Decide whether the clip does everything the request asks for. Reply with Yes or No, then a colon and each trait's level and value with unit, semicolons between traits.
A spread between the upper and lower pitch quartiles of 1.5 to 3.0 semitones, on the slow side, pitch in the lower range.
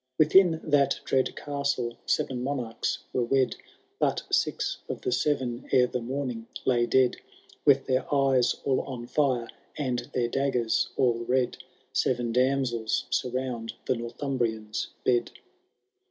Yes: narrow, 2.4 semitones; slow, 130 wpm; low, 125 Hz